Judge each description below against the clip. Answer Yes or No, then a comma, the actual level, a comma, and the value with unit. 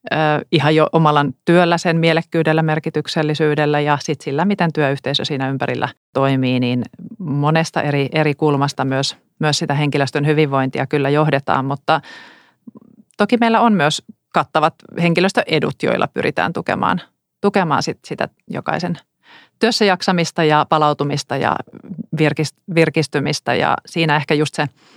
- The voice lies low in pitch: No, medium, 155 Hz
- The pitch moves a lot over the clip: No, average, 2.8 semitones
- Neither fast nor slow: Yes, average, 125 wpm